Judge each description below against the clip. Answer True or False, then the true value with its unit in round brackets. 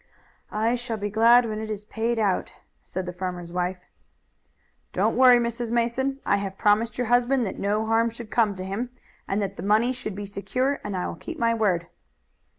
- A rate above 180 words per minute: True (200 wpm)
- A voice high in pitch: True (220 Hz)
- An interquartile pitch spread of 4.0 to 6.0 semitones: False (3.1 semitones)